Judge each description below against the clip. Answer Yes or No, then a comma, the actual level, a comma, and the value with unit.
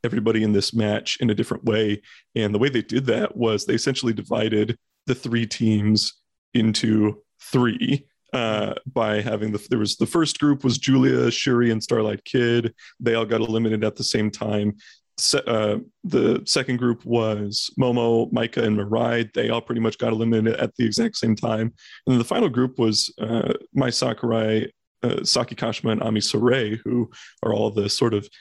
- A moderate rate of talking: Yes, average, 185 wpm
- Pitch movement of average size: No, narrow, 1.9 semitones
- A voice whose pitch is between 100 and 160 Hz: Yes, low, 115 Hz